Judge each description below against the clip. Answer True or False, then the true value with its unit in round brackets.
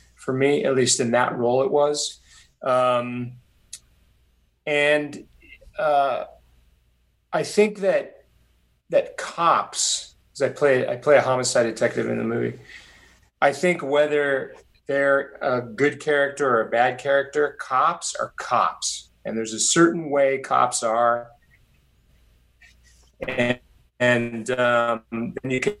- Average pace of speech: False (130 wpm)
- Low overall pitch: True (125 Hz)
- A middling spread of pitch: True (3.9 semitones)